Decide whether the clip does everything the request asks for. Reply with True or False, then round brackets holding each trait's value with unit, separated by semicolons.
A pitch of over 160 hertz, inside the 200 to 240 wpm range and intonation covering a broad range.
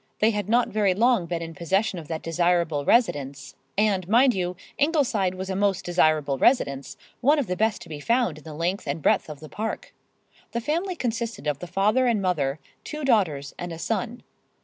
True (190 Hz; 205 wpm; 6.2 semitones)